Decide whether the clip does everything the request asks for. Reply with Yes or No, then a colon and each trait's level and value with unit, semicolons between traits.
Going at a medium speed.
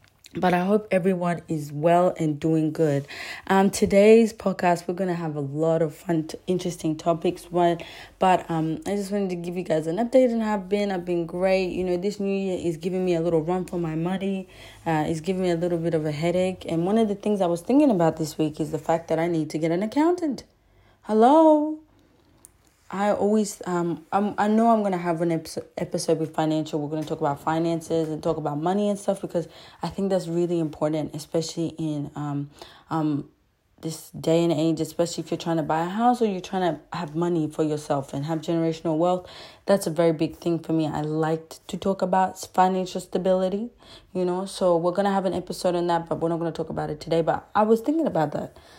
No: fast, 230 wpm